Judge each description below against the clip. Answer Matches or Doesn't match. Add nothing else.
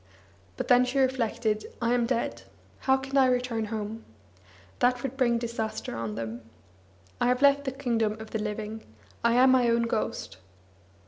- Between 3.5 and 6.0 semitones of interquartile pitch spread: Doesn't match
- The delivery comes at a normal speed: Matches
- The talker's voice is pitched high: Matches